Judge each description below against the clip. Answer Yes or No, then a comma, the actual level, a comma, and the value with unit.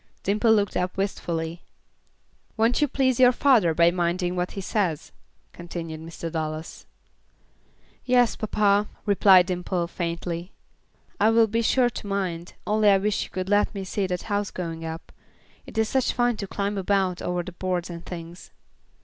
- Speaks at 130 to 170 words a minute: Yes, average, 165 wpm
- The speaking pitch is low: No, high, 190 Hz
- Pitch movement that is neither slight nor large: Yes, average, 3.6 semitones